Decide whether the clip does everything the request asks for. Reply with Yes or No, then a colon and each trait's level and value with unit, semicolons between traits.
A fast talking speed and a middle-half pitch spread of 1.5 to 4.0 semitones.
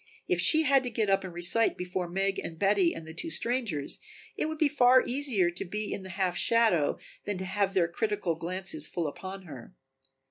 No: fast, 210 wpm; average, 4.8 semitones